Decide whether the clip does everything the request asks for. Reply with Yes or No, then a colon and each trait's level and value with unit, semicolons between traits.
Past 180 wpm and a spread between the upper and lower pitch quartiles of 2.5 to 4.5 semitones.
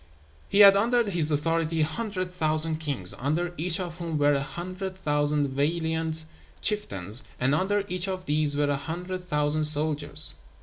No: average, 165 wpm; average, 3.7 semitones